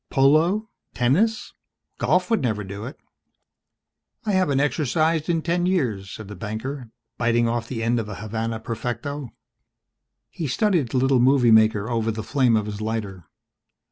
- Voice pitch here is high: No, low, 120 Hz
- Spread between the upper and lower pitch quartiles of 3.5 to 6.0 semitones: Yes, average, 5.1 semitones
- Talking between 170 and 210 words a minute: No, average, 155 wpm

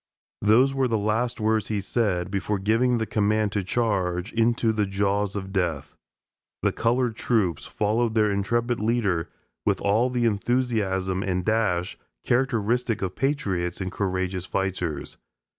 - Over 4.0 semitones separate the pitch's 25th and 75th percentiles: No, average, 3.5 semitones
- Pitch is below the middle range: Yes, low, 105 Hz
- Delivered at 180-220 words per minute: No, average, 140 wpm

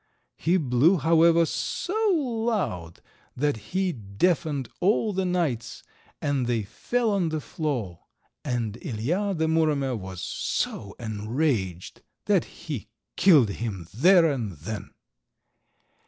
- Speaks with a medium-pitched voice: Yes, medium, 145 Hz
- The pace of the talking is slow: Yes, slow, 115 wpm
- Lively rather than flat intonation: Yes, wide, 8.1 semitones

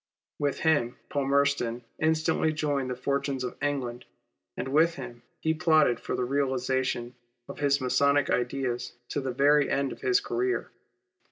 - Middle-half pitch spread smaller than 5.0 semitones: Yes, average, 2.9 semitones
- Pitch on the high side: No, medium, 140 Hz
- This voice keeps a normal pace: Yes, average, 150 wpm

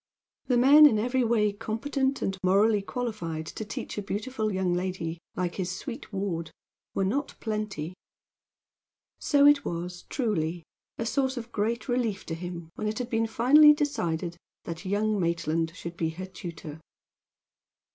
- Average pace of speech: Yes, average, 155 wpm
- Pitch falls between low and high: No, high, 205 Hz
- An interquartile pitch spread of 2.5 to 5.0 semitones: No, wide, 5.5 semitones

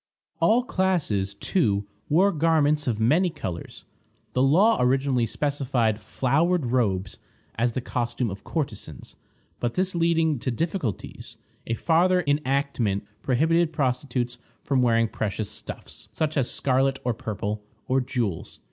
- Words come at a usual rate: No, slow, 130 wpm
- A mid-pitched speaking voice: No, low, 130 Hz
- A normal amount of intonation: No, wide, 5.7 semitones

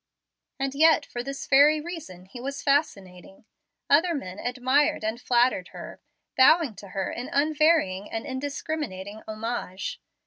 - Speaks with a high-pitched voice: Yes, very high, 260 Hz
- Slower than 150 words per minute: Yes, slow, 135 wpm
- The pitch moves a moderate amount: No, wide, 5.7 semitones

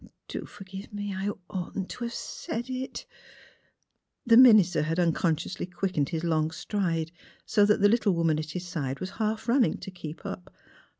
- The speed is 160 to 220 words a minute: Yes, average, 175 wpm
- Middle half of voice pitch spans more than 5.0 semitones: No, average, 4.3 semitones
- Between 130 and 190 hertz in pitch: Yes, medium, 185 Hz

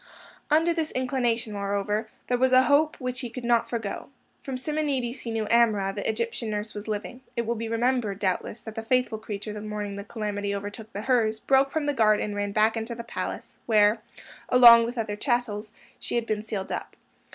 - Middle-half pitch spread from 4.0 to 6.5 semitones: No, average, 3.1 semitones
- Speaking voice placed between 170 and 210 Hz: No, high, 225 Hz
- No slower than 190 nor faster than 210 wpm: Yes, fast, 205 wpm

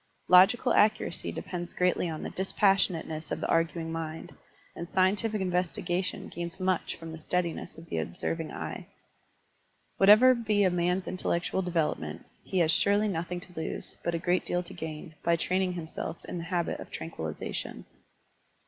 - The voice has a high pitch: No, medium, 175 Hz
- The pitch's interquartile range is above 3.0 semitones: No, narrow, 2.4 semitones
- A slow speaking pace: No, average, 165 wpm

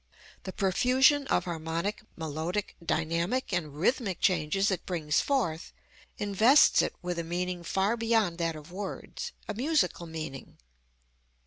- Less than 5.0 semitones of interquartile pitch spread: Yes, average, 4.5 semitones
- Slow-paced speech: Yes, slow, 130 wpm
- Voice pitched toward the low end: No, medium, 180 Hz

